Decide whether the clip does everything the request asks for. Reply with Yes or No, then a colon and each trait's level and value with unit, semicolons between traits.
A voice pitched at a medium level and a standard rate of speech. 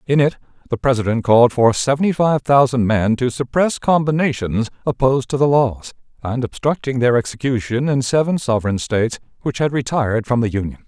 No: low, 125 Hz; average, 170 wpm